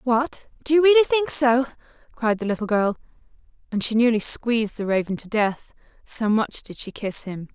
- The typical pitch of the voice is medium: No, high, 235 Hz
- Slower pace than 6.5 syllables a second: Yes, 5.0 syllables/s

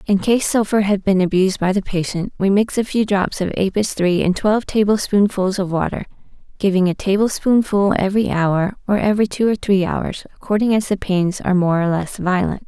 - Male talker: No, female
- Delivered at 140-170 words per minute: No, average, 200 wpm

